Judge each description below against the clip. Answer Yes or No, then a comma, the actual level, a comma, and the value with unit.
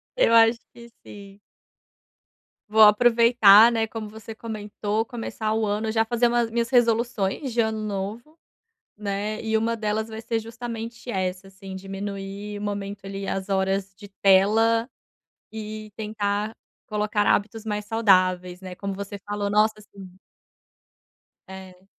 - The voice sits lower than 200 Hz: No, high, 210 Hz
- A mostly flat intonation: Yes, narrow, 2.2 semitones